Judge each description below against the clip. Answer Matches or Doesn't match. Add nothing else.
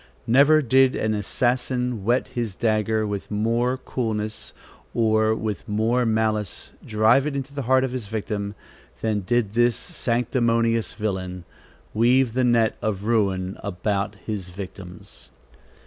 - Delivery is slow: Matches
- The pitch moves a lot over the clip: Doesn't match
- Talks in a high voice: Doesn't match